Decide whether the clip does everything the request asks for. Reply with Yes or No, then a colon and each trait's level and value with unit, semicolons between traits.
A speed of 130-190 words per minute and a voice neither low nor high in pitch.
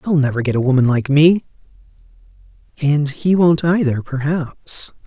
Yes: average, 140 wpm; medium, 145 Hz